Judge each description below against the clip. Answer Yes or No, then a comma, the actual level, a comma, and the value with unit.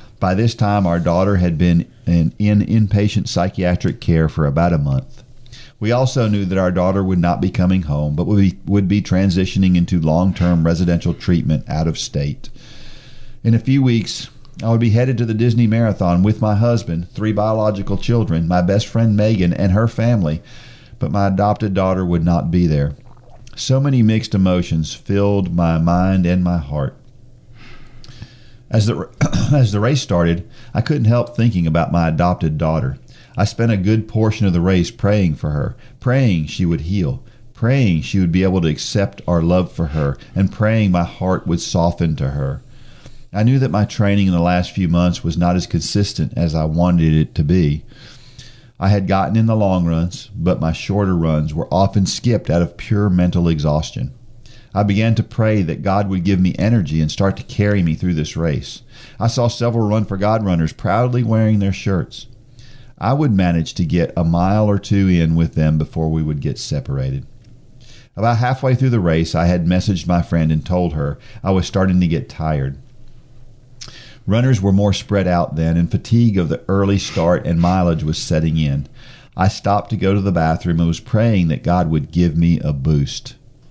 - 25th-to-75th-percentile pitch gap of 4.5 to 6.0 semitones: Yes, wide, 5.4 semitones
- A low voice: Yes, low, 100 Hz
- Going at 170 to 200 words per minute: Yes, average, 190 wpm